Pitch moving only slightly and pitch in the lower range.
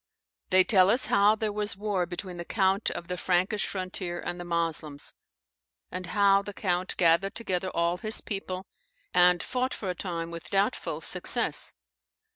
No: narrow, 2.3 semitones; medium, 185 Hz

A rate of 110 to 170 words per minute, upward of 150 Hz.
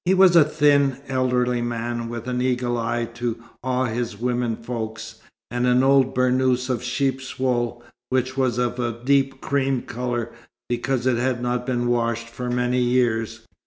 No: average, 165 wpm; low, 125 Hz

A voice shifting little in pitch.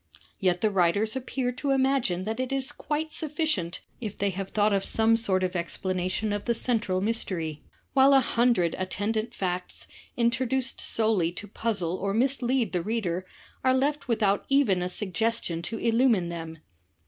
No: average, 5.2 semitones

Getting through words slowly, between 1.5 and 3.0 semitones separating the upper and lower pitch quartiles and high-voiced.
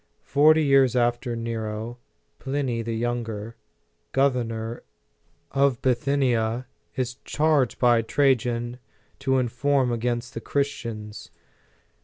No: slow, 95 wpm; narrow, 2.6 semitones; low, 120 Hz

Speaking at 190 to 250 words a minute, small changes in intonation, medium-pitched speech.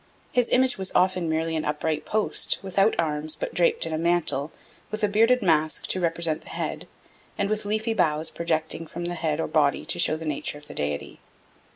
No: fast, 205 wpm; average, 3.9 semitones; medium, 165 Hz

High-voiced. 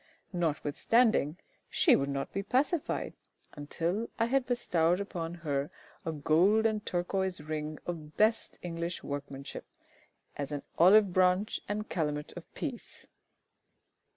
No: medium, 175 Hz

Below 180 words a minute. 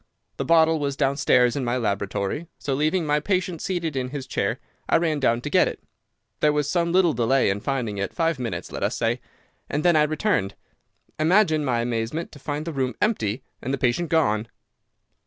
No: average, 190 wpm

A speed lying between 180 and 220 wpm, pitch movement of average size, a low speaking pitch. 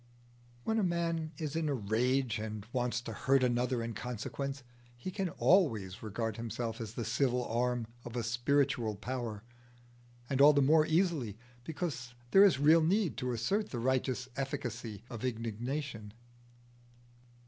No: average, 150 wpm; average, 4.2 semitones; low, 125 Hz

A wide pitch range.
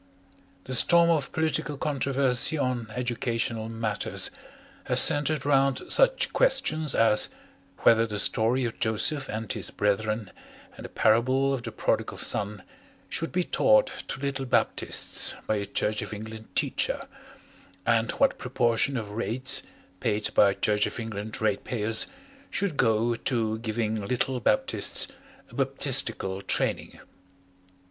No: average, 4.0 semitones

